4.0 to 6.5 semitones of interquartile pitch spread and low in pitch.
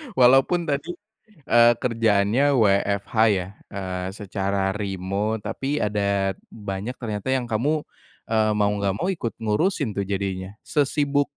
Yes: average, 4.8 semitones; low, 105 Hz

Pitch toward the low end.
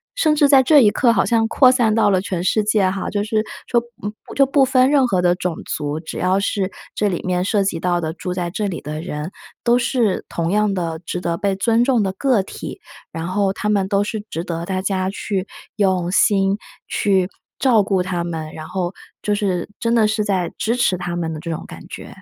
No: high, 195 Hz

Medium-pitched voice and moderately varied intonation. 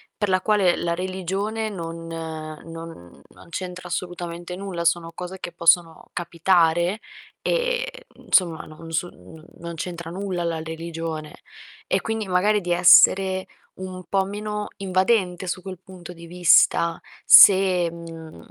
No: medium, 175 Hz; narrow, 2.3 semitones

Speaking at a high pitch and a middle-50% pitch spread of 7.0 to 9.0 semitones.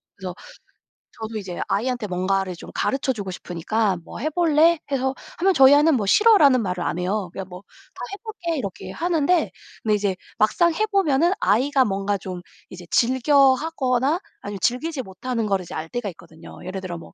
Yes: high, 235 Hz; wide, 7.4 semitones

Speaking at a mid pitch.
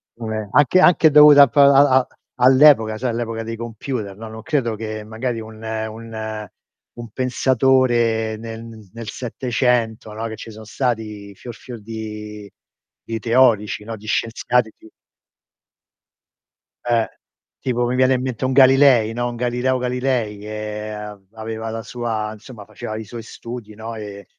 No: low, 115 Hz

